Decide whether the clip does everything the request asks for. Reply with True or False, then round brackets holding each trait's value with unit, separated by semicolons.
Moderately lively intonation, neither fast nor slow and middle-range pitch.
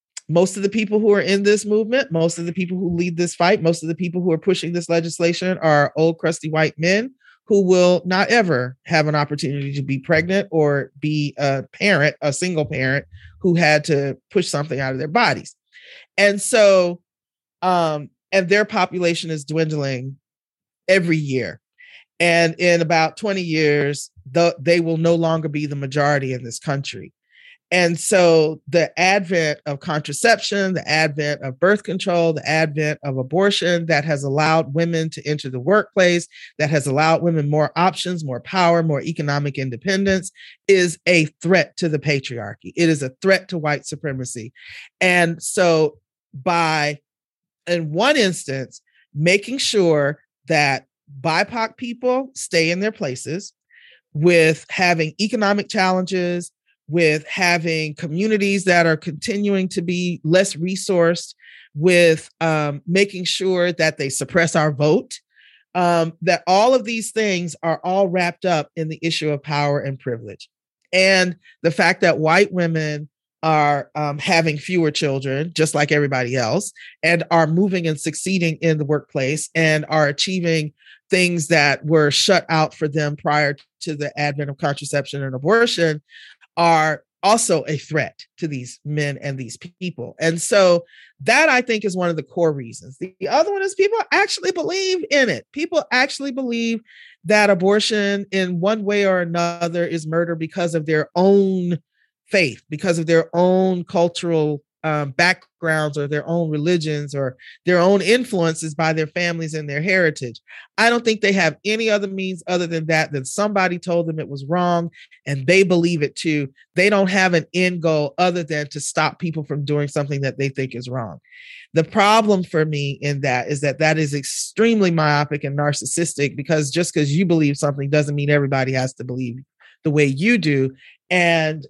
True (3.9 semitones; 170 wpm; 165 Hz)